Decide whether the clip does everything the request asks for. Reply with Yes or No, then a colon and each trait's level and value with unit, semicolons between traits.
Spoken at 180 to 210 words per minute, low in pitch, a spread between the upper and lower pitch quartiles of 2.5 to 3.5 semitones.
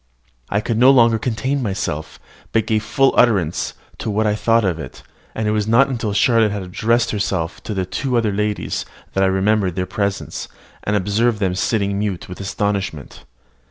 Yes: average, 185 wpm; low, 105 Hz; average, 3.0 semitones